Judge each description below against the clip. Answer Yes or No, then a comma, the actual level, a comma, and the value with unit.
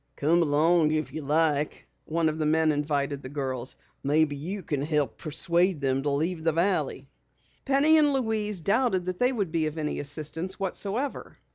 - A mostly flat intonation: No, average, 4.3 semitones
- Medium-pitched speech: Yes, medium, 160 Hz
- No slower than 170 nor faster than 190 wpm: Yes, average, 175 wpm